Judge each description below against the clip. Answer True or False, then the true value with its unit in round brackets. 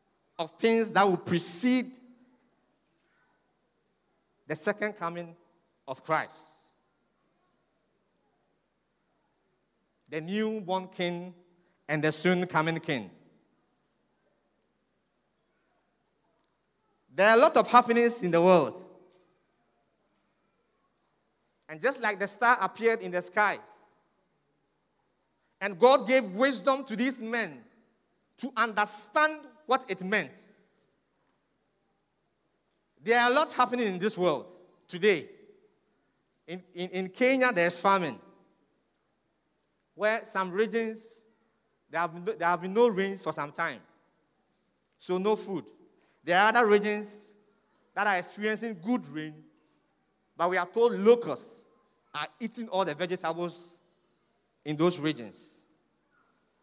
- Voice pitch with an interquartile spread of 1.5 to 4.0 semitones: False (4.6 semitones)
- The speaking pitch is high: True (200 Hz)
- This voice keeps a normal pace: False (110 wpm)